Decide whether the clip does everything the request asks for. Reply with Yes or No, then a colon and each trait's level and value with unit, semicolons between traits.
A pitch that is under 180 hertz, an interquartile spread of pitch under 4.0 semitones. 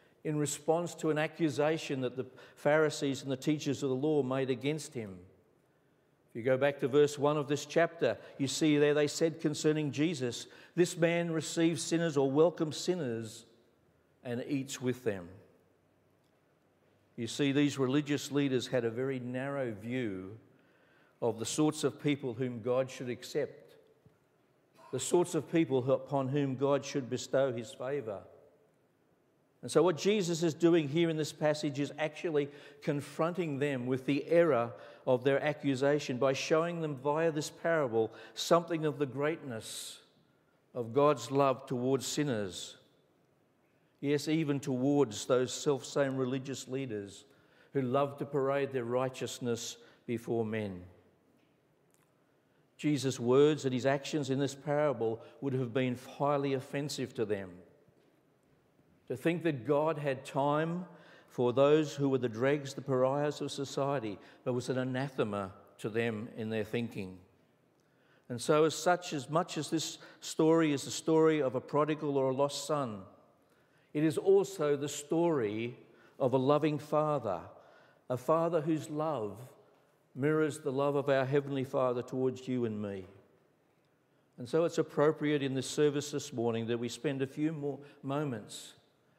Yes: medium, 140 Hz; average, 3.1 semitones